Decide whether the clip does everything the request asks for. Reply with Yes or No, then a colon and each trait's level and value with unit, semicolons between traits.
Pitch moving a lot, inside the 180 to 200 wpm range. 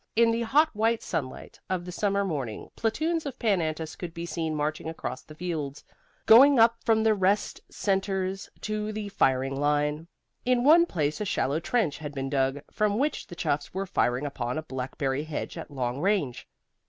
Yes: wide, 6.8 semitones; average, 185 wpm